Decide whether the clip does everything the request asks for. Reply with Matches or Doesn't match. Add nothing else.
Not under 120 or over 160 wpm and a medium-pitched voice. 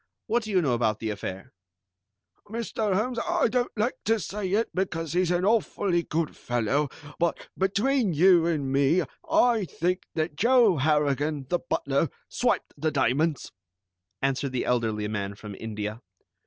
Matches